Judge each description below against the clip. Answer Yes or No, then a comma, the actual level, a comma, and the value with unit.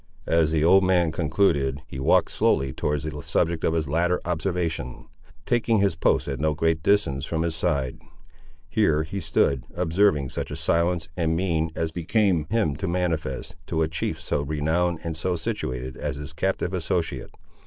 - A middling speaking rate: Yes, average, 175 wpm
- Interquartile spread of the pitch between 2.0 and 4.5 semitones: Yes, average, 3.0 semitones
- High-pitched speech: No, very low, 80 Hz